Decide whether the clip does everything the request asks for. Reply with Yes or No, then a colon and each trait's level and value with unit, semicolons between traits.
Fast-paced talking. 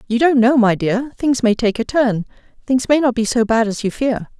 Yes: fast, 230 wpm